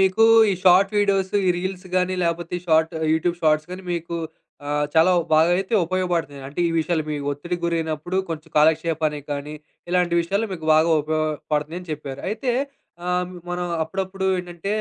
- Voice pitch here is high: No, medium, 170 Hz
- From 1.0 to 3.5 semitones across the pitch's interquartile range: Yes, average, 2.8 semitones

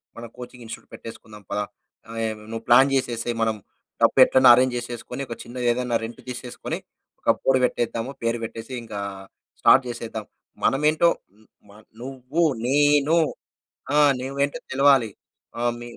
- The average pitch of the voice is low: Yes, low, 120 Hz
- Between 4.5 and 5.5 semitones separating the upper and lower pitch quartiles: No, narrow, 2.6 semitones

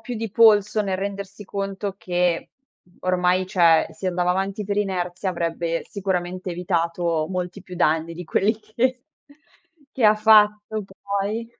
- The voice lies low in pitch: No, high, 190 Hz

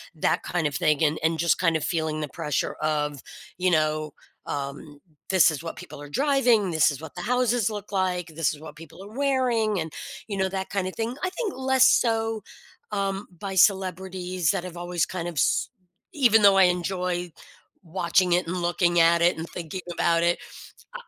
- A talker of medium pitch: Yes, medium, 180 Hz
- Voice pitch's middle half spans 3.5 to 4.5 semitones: Yes, average, 4.0 semitones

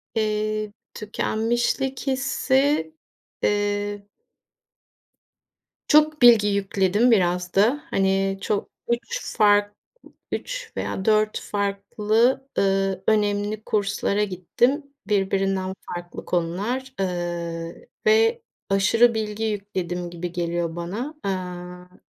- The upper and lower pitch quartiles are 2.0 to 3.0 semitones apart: No, average, 3.5 semitones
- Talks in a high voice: Yes, high, 205 Hz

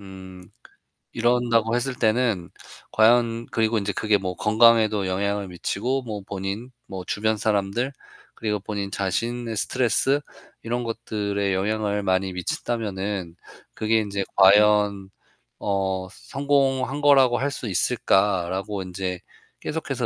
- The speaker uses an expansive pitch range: No, average, 3.3 semitones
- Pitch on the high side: No, low, 105 Hz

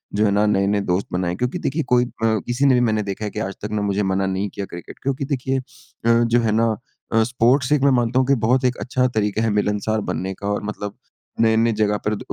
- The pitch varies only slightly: No, average, 3.3 semitones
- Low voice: Yes, low, 110 Hz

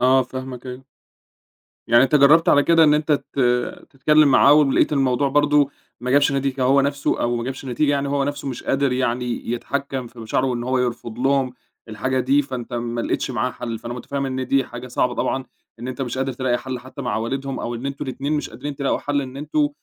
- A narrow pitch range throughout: Yes, narrow, 2.1 semitones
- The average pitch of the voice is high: No, low, 130 Hz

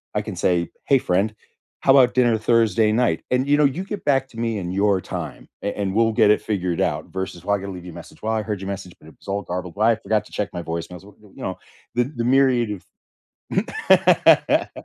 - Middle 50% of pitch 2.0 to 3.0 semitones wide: No, average, 4.3 semitones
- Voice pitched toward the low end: Yes, low, 105 Hz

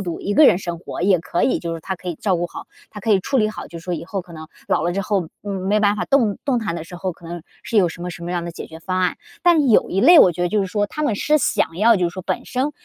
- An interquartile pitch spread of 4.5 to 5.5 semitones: No, average, 3.6 semitones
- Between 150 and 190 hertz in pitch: Yes, medium, 185 Hz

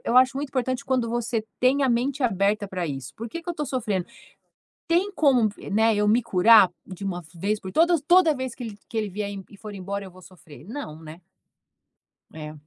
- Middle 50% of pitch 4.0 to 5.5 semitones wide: Yes, average, 5.2 semitones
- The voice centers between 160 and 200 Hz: No, high, 220 Hz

